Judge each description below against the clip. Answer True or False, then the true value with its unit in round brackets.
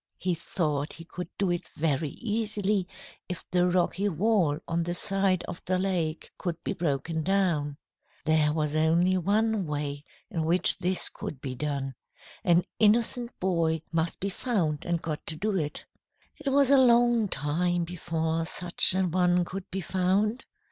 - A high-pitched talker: False (175 Hz)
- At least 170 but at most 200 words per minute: False (160 wpm)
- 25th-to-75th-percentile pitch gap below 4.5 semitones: True (3.5 semitones)